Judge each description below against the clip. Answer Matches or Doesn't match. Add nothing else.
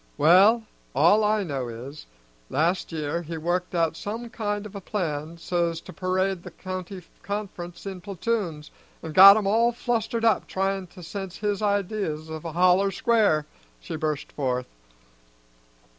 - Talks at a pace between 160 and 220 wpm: Doesn't match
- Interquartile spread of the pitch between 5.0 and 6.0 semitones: Doesn't match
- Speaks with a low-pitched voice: Doesn't match